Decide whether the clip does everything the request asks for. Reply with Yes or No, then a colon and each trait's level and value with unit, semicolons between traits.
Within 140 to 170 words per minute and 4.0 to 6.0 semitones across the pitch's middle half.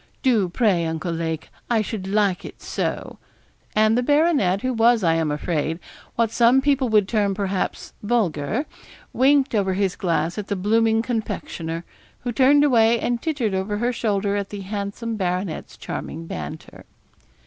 Yes: average, 160 wpm; average, 4.3 semitones